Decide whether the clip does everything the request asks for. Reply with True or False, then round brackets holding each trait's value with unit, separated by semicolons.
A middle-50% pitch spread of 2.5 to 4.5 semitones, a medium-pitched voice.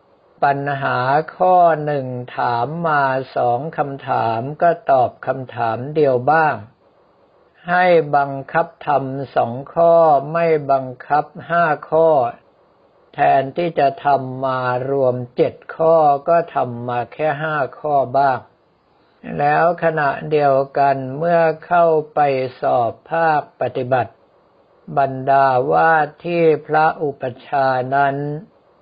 True (3.6 semitones; 145 Hz)